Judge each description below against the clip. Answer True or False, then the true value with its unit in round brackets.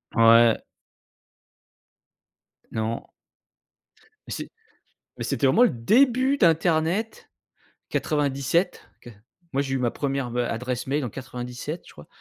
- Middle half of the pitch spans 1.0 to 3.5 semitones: False (5.5 semitones)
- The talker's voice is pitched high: False (135 Hz)